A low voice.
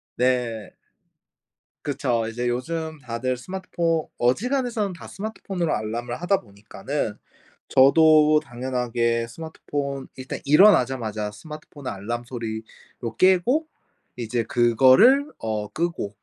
Yes: low, 130 Hz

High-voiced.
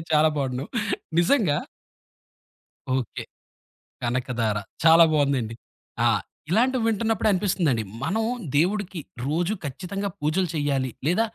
No: medium, 160 Hz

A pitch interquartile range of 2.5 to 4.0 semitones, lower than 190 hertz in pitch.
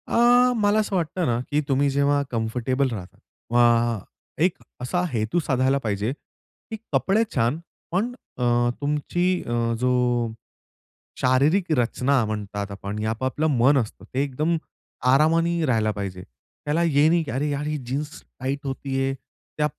No: average, 4.5 semitones; low, 135 Hz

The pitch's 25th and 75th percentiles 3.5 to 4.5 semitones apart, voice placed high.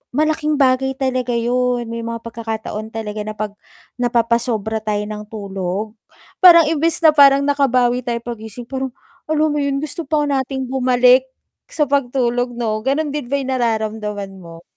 Yes: average, 3.8 semitones; high, 245 Hz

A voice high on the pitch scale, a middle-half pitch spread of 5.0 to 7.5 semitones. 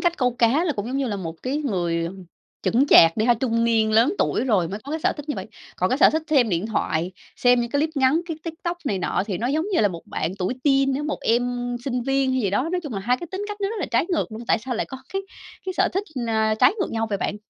Yes: high, 245 Hz; average, 5.3 semitones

